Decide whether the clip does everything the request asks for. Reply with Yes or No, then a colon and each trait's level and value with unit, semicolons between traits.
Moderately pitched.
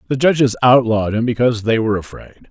No: low, 120 Hz